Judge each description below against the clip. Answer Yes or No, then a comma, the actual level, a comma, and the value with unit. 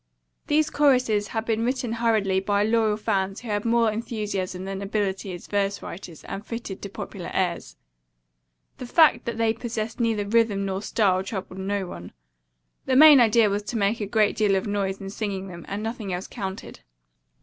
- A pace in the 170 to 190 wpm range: Yes, average, 180 wpm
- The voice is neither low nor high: No, high, 210 Hz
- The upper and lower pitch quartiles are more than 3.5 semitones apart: No, average, 2.9 semitones